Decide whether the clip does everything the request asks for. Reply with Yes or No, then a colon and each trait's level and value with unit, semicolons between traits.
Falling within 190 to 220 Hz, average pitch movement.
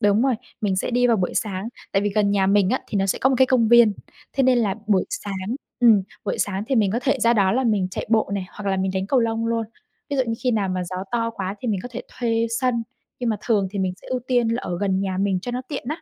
Yes: high, 215 Hz; average, 3.7 semitones